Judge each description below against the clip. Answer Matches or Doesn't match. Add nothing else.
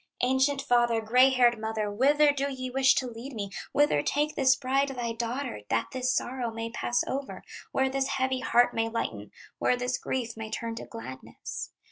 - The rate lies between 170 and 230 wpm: Matches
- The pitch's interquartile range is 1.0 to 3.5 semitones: Matches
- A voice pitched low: Doesn't match